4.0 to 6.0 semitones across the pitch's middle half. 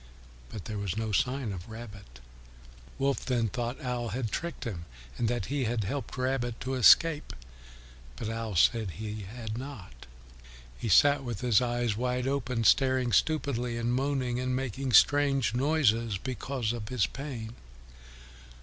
No: average, 3.2 semitones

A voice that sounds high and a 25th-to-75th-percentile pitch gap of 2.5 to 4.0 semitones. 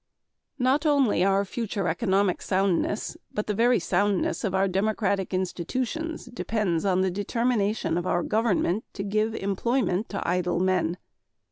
Yes: high, 200 Hz; average, 3.5 semitones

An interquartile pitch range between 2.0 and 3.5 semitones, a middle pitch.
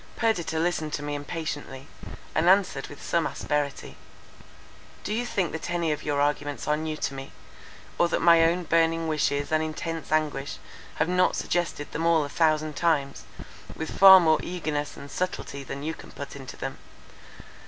Yes: narrow, 2.6 semitones; medium, 155 Hz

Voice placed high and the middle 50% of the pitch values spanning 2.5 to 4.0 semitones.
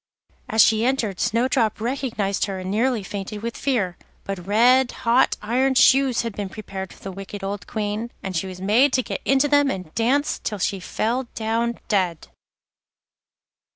No: high, 220 Hz; average, 4.4 semitones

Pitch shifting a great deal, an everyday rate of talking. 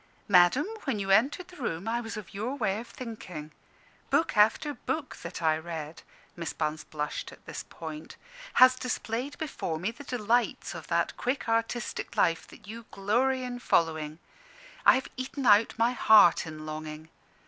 Yes: wide, 7.3 semitones; average, 170 wpm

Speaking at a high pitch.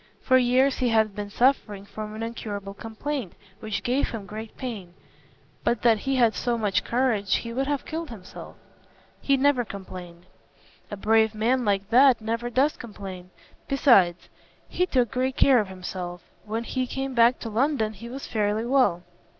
Yes: high, 225 Hz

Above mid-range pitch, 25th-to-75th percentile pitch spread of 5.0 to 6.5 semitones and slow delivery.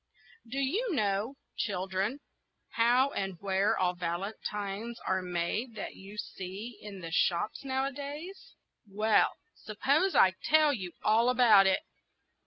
Yes: high, 210 Hz; wide, 5.5 semitones; slow, 130 wpm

